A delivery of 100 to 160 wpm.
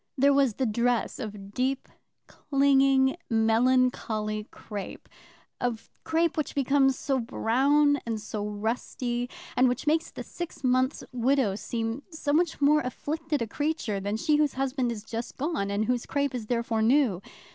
Yes: average, 155 wpm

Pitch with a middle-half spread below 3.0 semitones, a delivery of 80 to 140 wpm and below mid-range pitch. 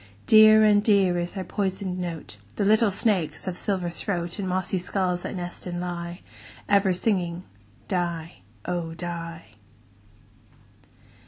No: narrow, 2.5 semitones; slow, 135 wpm; medium, 180 Hz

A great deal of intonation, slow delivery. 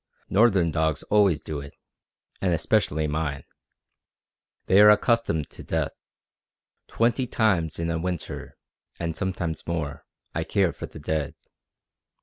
No: average, 4.3 semitones; slow, 130 wpm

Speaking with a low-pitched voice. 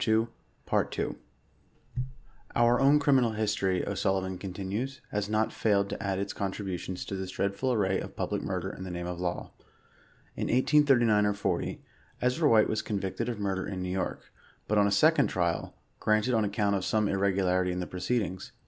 Yes: low, 100 Hz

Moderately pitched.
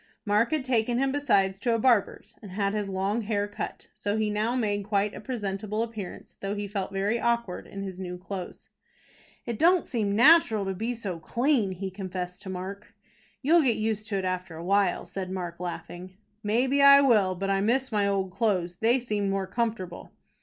No: high, 205 Hz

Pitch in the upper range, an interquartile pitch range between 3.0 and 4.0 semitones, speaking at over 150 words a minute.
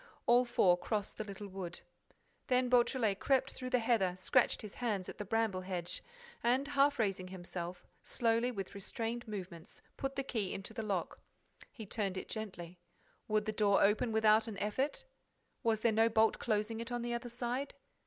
Yes: high, 220 Hz; average, 3.6 semitones; average, 180 wpm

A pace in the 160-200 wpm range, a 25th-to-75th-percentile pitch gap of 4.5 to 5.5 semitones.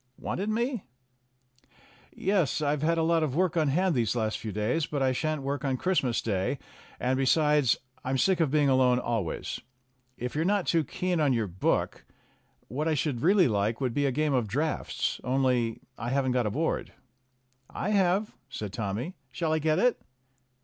Yes: average, 185 wpm; average, 4.9 semitones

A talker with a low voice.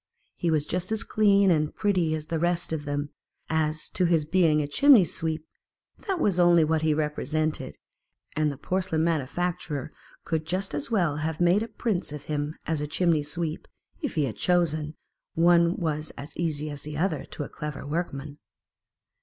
No: medium, 160 Hz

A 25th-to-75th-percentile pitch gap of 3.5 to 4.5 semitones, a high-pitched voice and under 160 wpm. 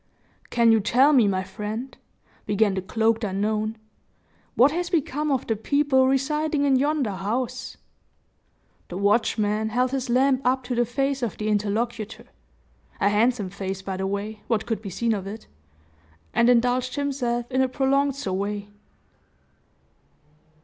Yes: average, 4.1 semitones; high, 235 Hz; average, 150 wpm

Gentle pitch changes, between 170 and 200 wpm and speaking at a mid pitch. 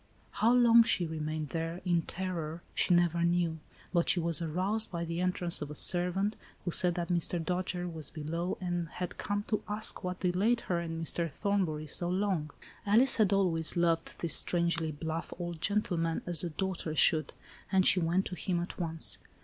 Yes: narrow, 2.2 semitones; average, 185 wpm; medium, 175 Hz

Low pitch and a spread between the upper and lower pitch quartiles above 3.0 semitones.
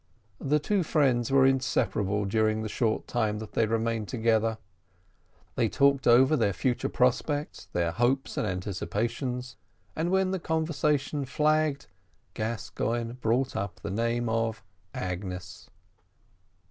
Yes: low, 120 Hz; average, 4.0 semitones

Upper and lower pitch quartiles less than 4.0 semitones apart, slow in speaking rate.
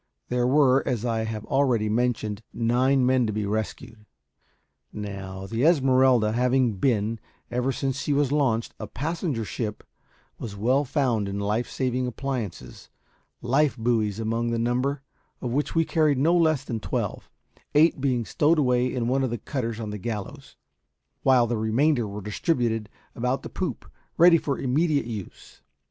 No: average, 3.6 semitones; average, 160 wpm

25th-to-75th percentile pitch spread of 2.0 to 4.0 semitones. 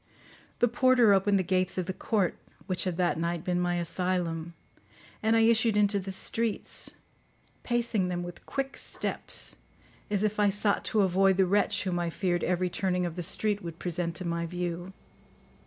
Yes: average, 2.8 semitones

